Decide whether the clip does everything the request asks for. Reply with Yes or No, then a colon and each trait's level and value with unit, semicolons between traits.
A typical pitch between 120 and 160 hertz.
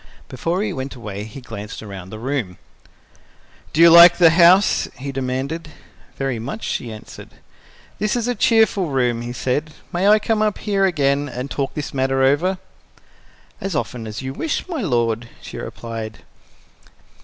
Yes: low, 135 Hz